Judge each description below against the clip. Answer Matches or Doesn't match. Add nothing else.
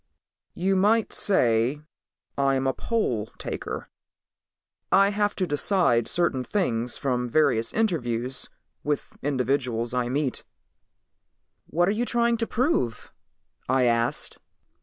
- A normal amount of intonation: Doesn't match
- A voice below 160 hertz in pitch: Matches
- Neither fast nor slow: Doesn't match